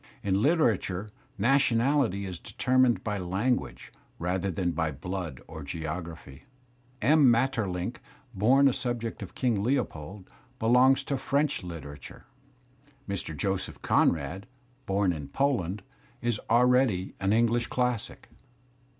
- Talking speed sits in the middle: No, slow, 120 wpm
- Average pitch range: No, wide, 5.8 semitones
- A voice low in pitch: Yes, low, 105 Hz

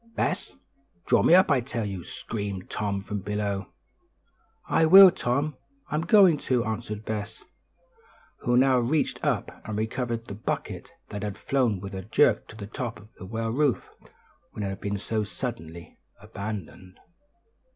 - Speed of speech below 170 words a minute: Yes, average, 160 wpm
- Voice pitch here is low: Yes, low, 110 Hz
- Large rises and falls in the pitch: No, average, 4.0 semitones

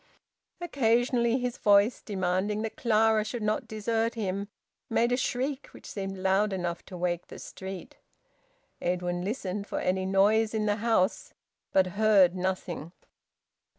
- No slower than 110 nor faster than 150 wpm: Yes, average, 140 wpm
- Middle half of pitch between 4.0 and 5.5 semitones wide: No, average, 3.2 semitones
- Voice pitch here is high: Yes, high, 205 Hz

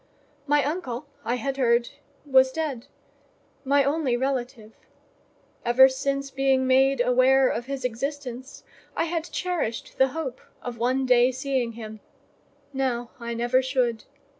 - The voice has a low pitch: No, very high, 260 Hz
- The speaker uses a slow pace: Yes, slow, 130 wpm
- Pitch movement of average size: No, narrow, 2.3 semitones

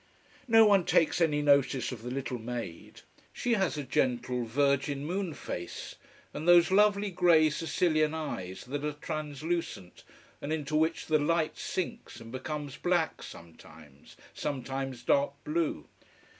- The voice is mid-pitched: Yes, medium, 150 Hz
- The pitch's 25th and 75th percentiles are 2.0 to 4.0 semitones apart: No, average, 4.4 semitones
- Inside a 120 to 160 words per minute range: Yes, average, 140 wpm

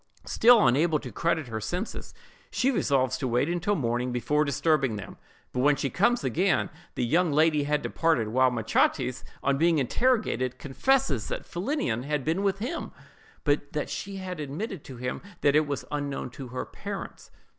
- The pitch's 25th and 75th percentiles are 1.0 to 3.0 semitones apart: No, wide, 5.5 semitones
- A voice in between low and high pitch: Yes, medium, 145 Hz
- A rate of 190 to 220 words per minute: No, average, 175 wpm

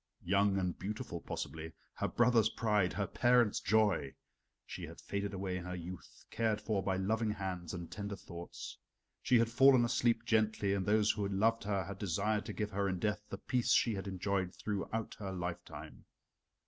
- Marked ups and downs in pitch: No, average, 2.7 semitones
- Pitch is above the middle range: No, low, 100 Hz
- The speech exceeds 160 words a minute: Yes, average, 180 wpm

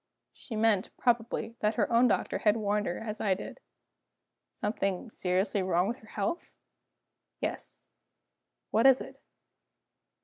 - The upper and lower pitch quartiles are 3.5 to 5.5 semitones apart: No, average, 2.7 semitones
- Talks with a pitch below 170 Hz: No, high, 215 Hz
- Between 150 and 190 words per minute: No, slow, 135 wpm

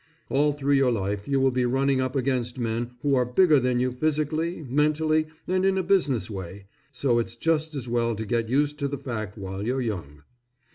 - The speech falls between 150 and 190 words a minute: No, fast, 205 wpm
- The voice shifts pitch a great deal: No, average, 4.0 semitones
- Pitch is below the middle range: Yes, low, 130 Hz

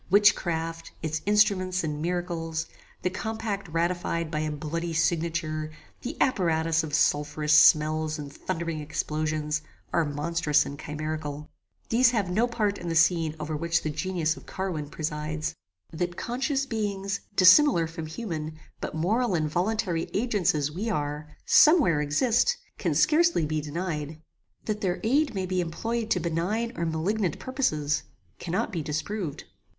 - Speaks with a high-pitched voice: No, medium, 170 Hz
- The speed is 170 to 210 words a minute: No, average, 145 wpm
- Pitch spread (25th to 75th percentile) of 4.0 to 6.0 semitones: Yes, average, 4.4 semitones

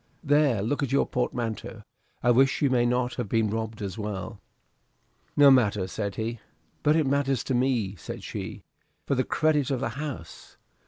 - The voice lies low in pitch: Yes, low, 125 Hz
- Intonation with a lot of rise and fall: No, average, 4.0 semitones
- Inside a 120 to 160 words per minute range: No, average, 175 wpm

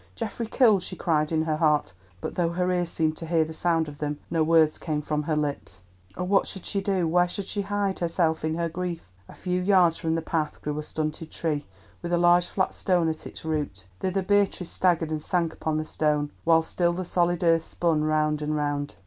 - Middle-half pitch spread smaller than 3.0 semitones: Yes, narrow, 2.6 semitones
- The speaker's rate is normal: No, fast, 225 wpm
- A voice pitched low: No, medium, 165 Hz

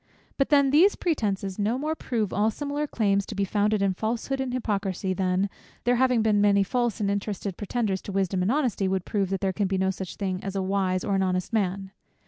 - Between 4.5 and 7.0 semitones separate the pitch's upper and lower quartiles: No, average, 3.7 semitones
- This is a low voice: No, high, 200 Hz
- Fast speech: Yes, fast, 225 wpm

